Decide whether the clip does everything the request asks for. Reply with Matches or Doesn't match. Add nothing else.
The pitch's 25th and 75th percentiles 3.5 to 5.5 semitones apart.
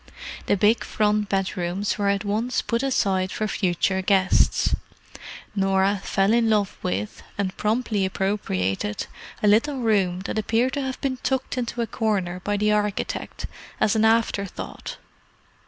Doesn't match